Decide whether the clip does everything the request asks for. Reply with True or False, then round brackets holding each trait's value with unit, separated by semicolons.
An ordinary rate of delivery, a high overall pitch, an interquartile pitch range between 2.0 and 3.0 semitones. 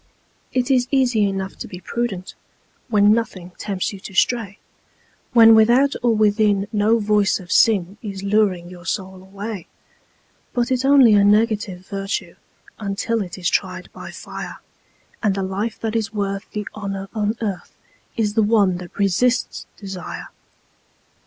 True (150 wpm; 205 Hz; 2.6 semitones)